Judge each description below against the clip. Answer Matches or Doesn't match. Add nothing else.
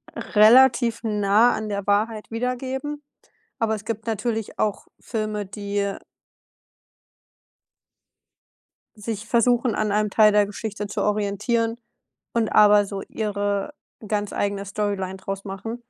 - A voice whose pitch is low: Doesn't match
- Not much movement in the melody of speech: Matches